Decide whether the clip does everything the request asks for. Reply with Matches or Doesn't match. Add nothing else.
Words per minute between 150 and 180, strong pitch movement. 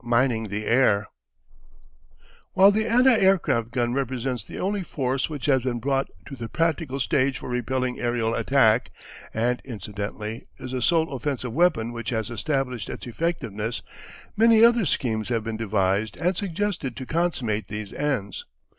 Matches